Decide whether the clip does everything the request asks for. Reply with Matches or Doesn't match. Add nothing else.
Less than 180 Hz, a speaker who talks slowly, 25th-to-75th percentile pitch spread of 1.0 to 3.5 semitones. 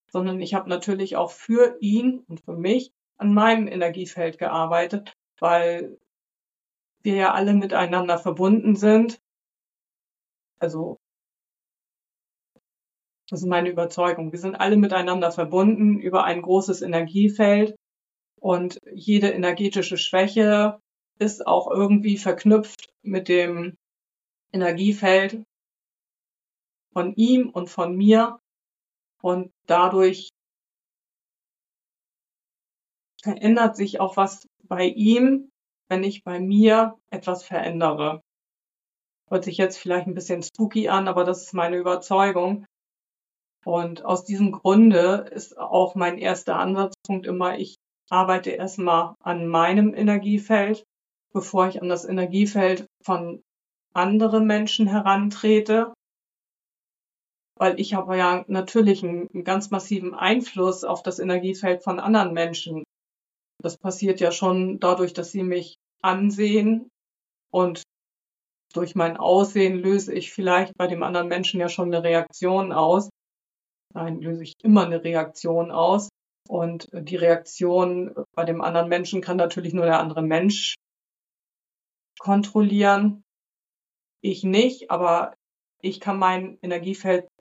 Doesn't match